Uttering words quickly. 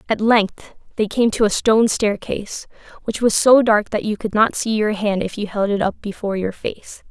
Yes: fast, 230 wpm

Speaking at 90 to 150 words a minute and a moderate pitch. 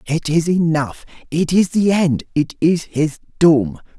Yes: slow, 135 wpm; medium, 160 Hz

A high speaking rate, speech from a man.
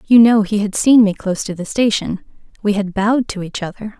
No: fast, 240 wpm; female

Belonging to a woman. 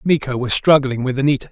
No: male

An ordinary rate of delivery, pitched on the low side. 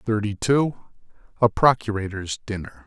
No: slow, 105 wpm; low, 110 Hz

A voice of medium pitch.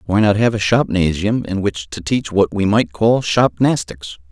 No: low, 100 Hz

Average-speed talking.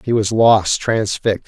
Yes: average, 165 wpm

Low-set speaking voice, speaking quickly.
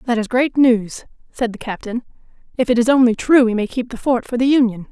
No: high, 240 Hz; fast, 245 wpm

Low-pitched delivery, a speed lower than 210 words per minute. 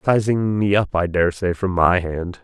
Yes: very low, 95 Hz; average, 200 wpm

